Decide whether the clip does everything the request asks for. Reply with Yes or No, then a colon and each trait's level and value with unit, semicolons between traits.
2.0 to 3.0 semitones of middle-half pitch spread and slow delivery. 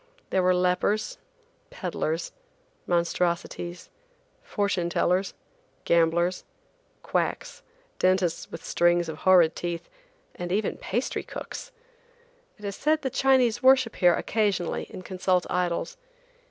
No: average, 3.7 semitones; slow, 110 wpm